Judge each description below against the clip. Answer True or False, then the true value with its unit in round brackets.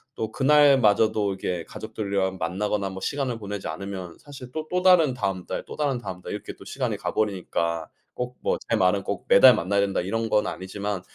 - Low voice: True (105 Hz)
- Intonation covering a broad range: False (4.7 semitones)